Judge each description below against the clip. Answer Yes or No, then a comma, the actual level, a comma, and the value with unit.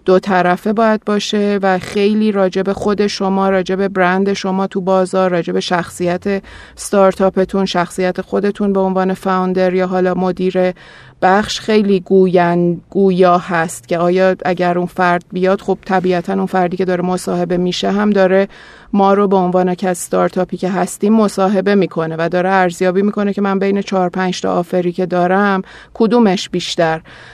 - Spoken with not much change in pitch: Yes, narrow, 1.5 semitones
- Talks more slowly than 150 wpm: No, fast, 155 wpm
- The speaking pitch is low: No, medium, 185 Hz